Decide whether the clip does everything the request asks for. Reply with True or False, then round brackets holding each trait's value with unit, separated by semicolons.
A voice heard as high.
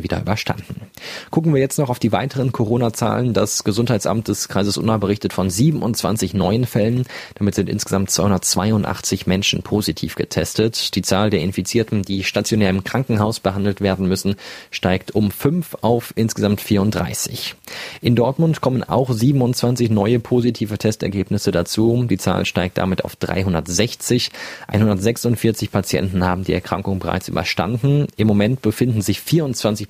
False (105 Hz)